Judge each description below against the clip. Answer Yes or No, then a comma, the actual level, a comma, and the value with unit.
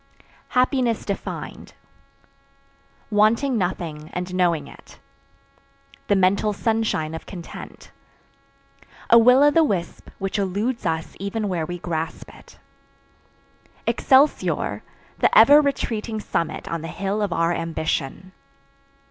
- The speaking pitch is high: Yes, high, 195 Hz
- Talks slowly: Yes, slow, 115 wpm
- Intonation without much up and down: No, average, 5.2 semitones